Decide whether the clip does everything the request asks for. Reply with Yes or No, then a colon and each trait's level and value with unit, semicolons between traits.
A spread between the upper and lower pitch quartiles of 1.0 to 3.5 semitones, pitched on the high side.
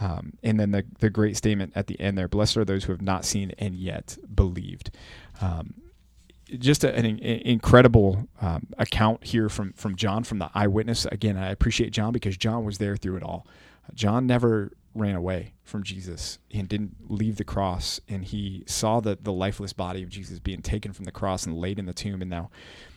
No: narrow, 2.6 semitones; low, 100 Hz